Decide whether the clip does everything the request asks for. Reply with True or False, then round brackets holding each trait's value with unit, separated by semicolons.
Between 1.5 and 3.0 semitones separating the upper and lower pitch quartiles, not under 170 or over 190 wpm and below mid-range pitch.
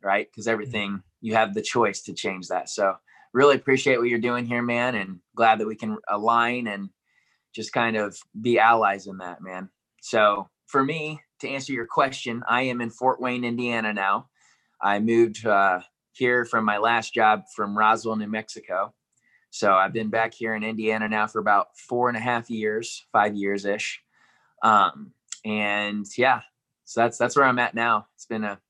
True (2.6 semitones; 185 wpm; 110 Hz)